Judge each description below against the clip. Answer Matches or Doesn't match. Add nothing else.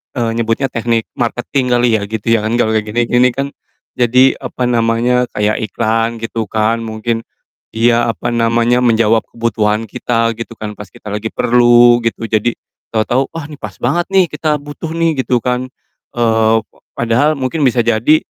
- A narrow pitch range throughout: Matches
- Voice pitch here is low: Matches